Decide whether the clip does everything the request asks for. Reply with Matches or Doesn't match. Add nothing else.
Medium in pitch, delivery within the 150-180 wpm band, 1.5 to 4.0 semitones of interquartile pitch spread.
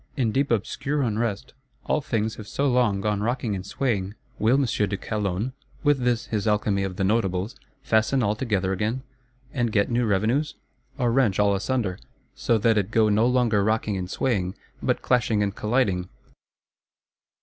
Doesn't match